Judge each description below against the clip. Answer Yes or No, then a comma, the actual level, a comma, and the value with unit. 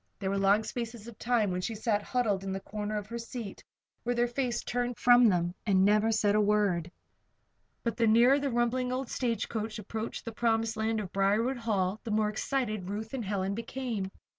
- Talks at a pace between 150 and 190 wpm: No, average, 200 wpm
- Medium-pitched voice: No, high, 220 Hz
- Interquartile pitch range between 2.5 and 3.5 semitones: Yes, average, 2.8 semitones